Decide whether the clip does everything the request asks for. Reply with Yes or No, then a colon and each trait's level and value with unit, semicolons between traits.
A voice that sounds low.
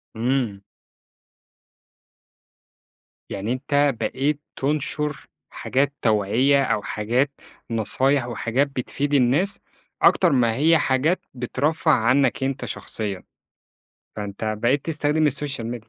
Yes: low, 130 Hz